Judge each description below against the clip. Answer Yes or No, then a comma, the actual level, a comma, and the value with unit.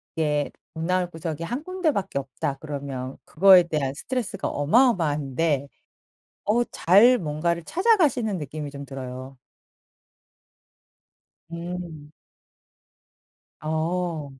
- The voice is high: No, medium, 160 Hz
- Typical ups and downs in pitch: Yes, average, 5.0 semitones